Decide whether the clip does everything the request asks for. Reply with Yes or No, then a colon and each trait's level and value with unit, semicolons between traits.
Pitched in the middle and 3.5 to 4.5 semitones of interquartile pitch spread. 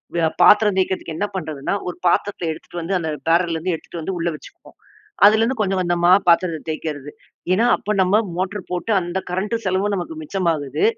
No: medium, 180 Hz; average, 3.1 semitones